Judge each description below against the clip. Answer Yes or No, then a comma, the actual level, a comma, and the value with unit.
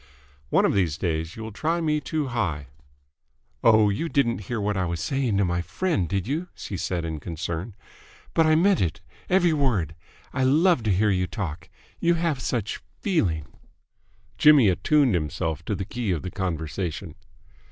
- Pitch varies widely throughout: Yes, wide, 8.9 semitones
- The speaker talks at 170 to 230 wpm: Yes, average, 180 wpm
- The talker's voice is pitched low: Yes, low, 100 Hz